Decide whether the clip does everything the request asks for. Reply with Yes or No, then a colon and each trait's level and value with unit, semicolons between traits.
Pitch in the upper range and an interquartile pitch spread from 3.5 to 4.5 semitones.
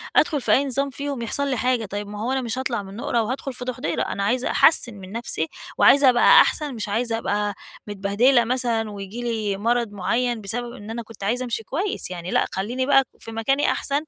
Yes: high, 235 Hz; average, 3.8 semitones